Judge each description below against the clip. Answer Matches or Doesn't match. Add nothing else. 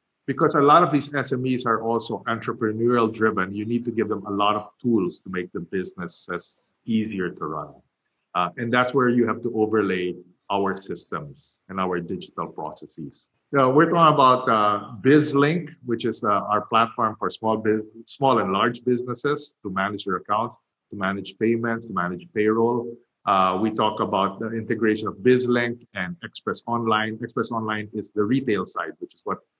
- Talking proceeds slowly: Doesn't match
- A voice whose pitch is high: Doesn't match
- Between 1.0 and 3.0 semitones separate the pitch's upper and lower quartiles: Matches